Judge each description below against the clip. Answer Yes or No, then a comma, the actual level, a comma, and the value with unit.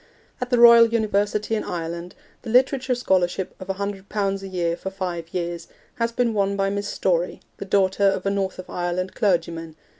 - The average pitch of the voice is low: No, high, 195 Hz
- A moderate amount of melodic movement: Yes, average, 3.0 semitones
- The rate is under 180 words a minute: No, average, 185 wpm